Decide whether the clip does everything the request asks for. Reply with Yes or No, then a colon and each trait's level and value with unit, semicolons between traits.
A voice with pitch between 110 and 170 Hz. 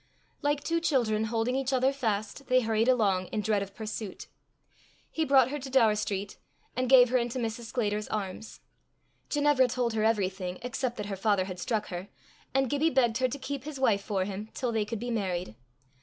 No: high, 225 Hz